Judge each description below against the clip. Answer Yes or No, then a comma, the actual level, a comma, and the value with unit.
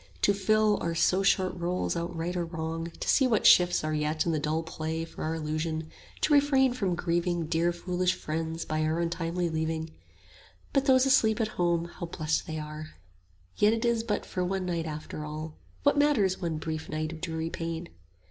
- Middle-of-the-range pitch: Yes, medium, 170 Hz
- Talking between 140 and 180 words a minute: No, average, 200 wpm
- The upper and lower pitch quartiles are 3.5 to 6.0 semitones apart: No, average, 3.0 semitones